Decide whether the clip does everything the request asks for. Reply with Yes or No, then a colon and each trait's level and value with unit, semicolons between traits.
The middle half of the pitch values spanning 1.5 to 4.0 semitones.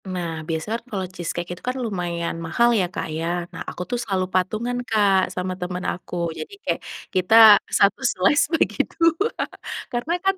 No: wide, 5.4 semitones